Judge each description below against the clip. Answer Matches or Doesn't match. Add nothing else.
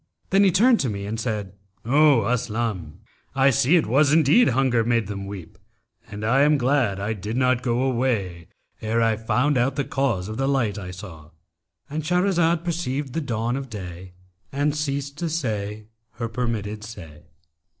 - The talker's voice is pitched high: Doesn't match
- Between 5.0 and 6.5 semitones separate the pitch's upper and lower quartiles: Matches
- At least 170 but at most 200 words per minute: Matches